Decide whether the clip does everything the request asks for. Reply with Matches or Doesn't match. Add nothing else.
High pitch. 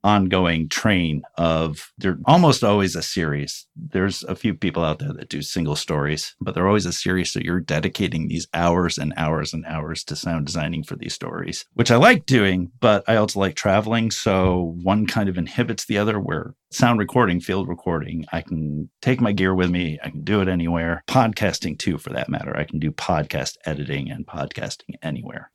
Doesn't match